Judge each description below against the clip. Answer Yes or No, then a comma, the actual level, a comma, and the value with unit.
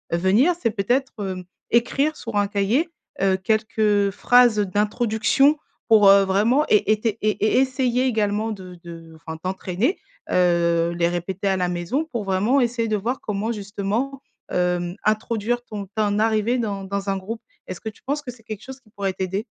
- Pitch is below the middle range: No, high, 210 Hz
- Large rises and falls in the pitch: No, average, 3.7 semitones